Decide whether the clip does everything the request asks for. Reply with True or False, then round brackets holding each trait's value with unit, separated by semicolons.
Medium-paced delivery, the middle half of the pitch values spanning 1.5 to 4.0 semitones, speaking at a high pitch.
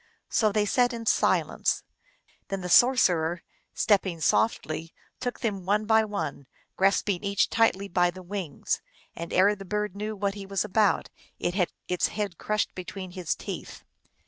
True (160 wpm; 2.8 semitones; 195 Hz)